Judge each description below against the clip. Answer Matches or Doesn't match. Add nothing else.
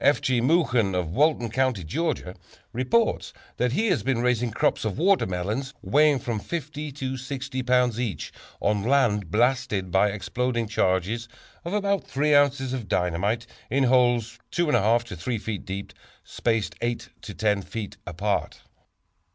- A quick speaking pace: Doesn't match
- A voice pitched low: Matches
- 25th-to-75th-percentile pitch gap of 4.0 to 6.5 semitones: Matches